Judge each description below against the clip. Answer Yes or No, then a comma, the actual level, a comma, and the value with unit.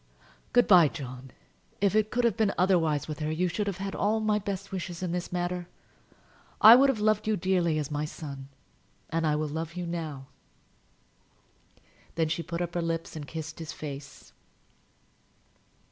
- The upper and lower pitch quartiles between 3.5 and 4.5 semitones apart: Yes, average, 4.2 semitones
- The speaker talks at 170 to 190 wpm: Yes, average, 175 wpm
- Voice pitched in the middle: Yes, medium, 170 Hz